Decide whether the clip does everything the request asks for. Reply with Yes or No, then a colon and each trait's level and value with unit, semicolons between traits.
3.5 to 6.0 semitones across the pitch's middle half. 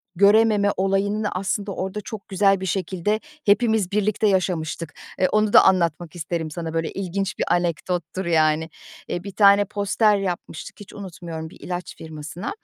No: average, 3.1 semitones